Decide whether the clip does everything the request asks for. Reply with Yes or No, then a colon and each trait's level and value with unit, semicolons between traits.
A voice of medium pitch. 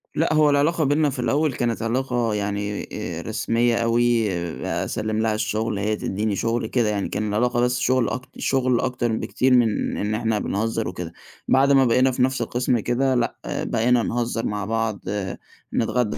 No: low, 115 Hz